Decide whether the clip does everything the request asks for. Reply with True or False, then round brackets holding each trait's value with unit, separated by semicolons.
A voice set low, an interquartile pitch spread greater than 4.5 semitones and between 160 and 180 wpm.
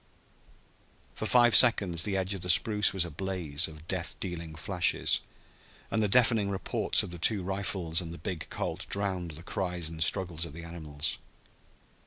False (90 Hz; 2.9 semitones; 175 wpm)